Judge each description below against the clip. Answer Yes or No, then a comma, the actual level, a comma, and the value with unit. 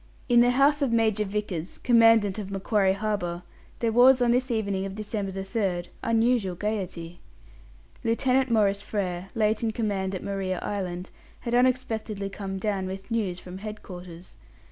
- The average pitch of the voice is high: Yes, high, 205 Hz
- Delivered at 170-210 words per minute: No, average, 155 wpm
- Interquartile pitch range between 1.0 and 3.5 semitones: Yes, average, 3.2 semitones